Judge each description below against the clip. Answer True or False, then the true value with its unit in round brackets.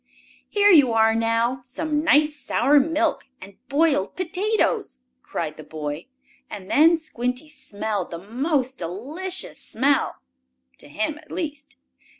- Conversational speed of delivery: False (130 wpm)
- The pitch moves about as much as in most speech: False (6.3 semitones)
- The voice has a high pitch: True (275 Hz)